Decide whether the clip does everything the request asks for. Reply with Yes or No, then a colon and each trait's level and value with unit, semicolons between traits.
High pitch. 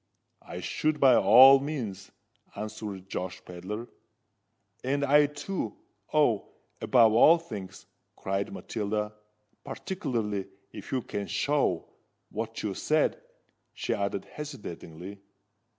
No: low, 110 Hz